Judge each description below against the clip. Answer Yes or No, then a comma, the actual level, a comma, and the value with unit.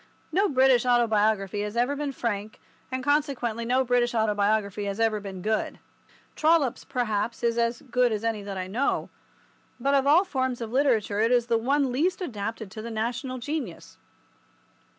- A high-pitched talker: Yes, high, 235 Hz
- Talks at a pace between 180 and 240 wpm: No, average, 170 wpm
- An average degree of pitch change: Yes, average, 3.5 semitones